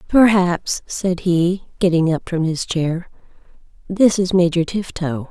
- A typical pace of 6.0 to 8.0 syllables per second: No, 3.8 syllables/s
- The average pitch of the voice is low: No, medium, 175 Hz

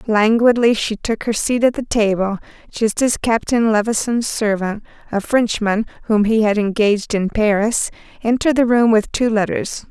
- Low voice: No, high, 220 Hz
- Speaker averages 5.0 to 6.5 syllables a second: No, 4.8 syllables/s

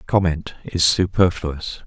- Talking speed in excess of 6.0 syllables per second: No, 3.8 syllables/s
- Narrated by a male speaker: Yes, male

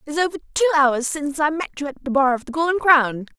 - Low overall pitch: No, very high, 295 Hz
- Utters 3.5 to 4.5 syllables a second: No, 6.8 syllables/s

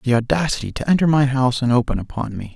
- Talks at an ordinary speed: No, fast, 235 wpm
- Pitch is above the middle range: No, low, 130 Hz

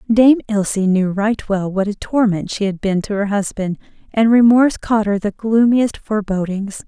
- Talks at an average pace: Yes, average, 185 wpm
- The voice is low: No, high, 210 Hz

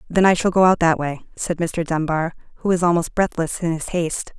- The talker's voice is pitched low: No, medium, 170 Hz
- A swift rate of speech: Yes, fast, 235 wpm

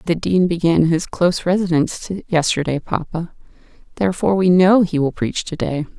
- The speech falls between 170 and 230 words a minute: No, average, 160 wpm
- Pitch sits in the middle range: Yes, medium, 170 Hz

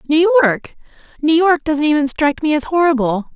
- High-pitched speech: Yes, very high, 290 Hz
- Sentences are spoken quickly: No, average, 160 wpm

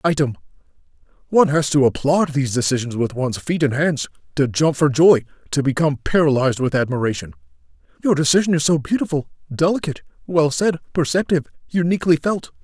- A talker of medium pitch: Yes, medium, 145 Hz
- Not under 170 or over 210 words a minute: No, average, 145 wpm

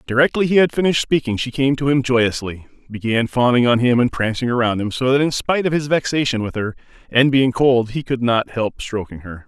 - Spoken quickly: Yes, fast, 230 wpm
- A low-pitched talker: Yes, low, 125 Hz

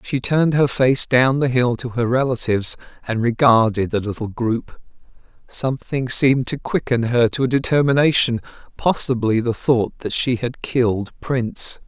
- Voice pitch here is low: Yes, low, 125 Hz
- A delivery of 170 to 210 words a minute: No, average, 155 wpm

